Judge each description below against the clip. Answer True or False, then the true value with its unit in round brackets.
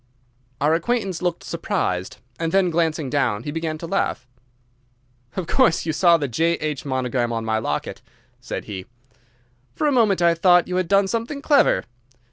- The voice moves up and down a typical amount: False (6.0 semitones)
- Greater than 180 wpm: False (165 wpm)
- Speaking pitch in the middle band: True (165 Hz)